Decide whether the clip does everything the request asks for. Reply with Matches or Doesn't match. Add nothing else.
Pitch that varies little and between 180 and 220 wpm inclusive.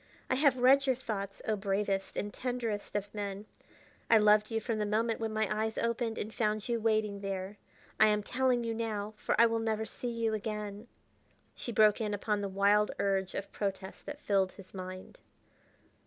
Matches